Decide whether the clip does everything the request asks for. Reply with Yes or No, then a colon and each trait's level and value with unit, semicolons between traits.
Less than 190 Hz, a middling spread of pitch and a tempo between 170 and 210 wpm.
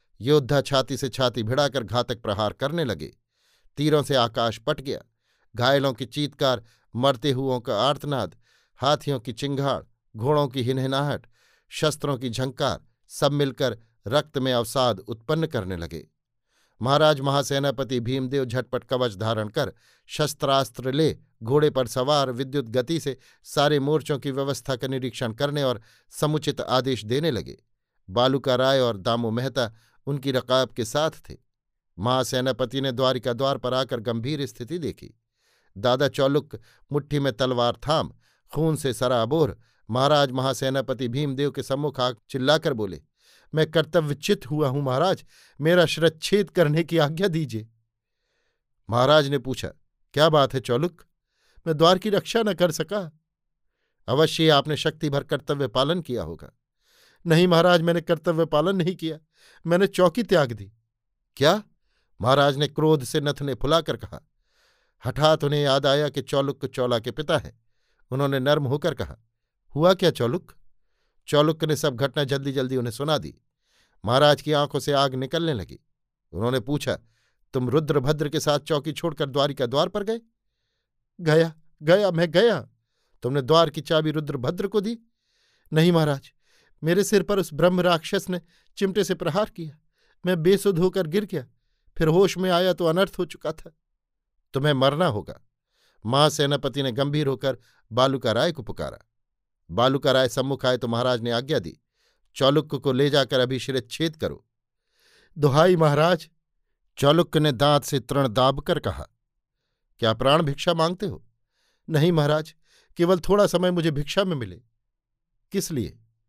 No: medium, 140 Hz; average, 3.8 semitones; average, 150 wpm